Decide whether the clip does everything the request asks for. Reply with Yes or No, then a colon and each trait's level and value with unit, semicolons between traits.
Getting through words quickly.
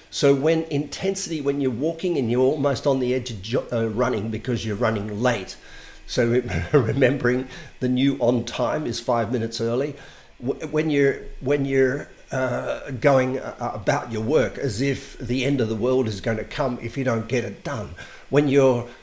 No: average, 175 wpm